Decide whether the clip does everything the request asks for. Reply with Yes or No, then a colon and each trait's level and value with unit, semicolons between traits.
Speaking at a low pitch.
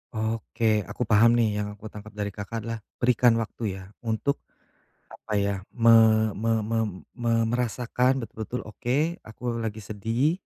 Yes: low, 115 Hz